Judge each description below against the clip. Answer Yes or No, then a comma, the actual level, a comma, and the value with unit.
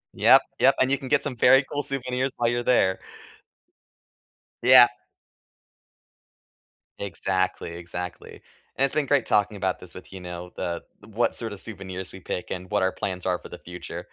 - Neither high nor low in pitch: No, low, 100 Hz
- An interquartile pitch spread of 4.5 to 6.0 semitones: Yes, wide, 5.6 semitones